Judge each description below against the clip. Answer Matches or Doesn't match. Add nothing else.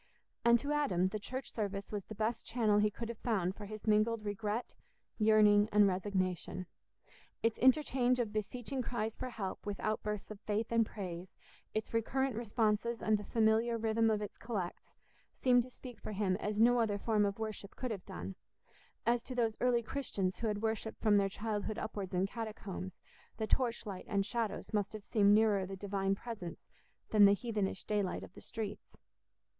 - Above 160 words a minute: Matches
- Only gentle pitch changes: Matches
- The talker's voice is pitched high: Matches